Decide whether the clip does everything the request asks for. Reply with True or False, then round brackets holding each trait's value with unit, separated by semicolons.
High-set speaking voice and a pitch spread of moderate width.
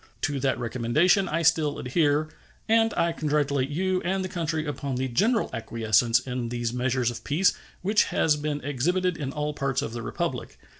False (145 Hz; 5.0 semitones)